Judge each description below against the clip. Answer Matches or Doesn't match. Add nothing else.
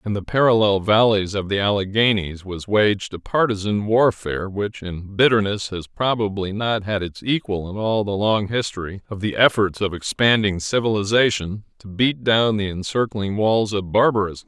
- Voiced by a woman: Doesn't match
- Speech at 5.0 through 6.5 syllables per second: Doesn't match